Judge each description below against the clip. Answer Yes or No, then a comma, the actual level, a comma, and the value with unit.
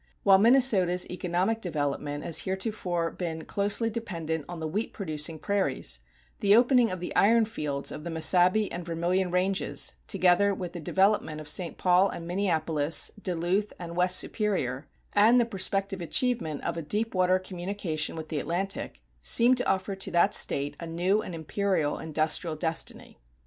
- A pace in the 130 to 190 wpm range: Yes, average, 160 wpm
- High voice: No, medium, 180 Hz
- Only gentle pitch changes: No, average, 3.7 semitones